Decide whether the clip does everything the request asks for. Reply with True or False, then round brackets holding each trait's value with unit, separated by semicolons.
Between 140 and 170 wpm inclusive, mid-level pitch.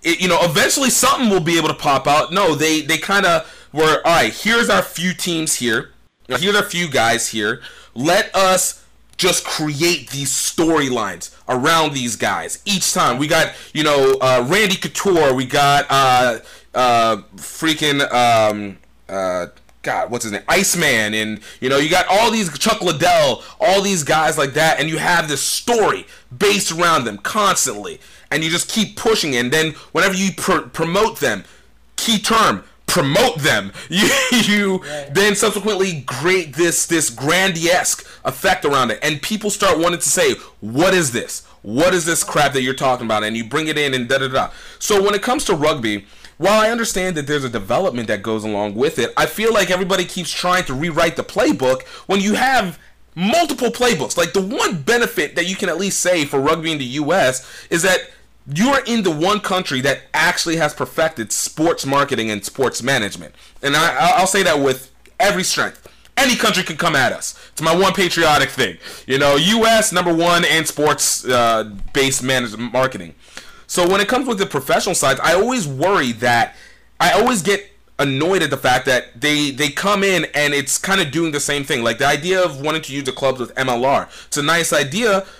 False (195 wpm; 160 Hz)